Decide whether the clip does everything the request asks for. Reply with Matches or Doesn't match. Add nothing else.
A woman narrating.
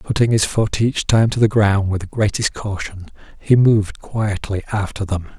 Doesn't match